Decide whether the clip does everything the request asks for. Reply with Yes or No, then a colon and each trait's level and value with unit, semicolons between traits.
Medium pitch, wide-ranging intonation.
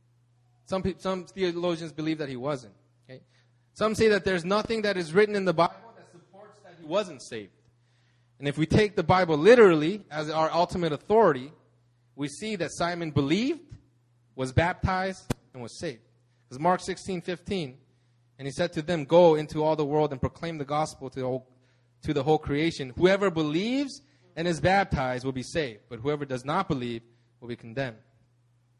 Yes: medium, 150 Hz; wide, 6.6 semitones